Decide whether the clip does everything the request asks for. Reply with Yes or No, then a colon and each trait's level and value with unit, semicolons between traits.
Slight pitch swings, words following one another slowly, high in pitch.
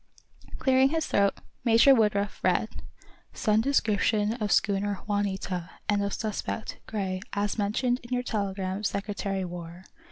Yes: narrow, 2.3 semitones; slow, 130 wpm; high, 205 Hz